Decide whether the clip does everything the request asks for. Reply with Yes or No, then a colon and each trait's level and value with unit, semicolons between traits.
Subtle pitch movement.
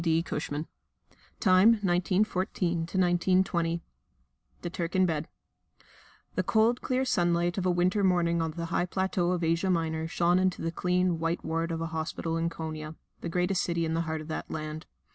Yes: narrow, 2.0 semitones